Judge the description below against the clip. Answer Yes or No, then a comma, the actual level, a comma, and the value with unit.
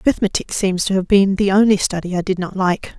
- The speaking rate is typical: No, fast, 240 wpm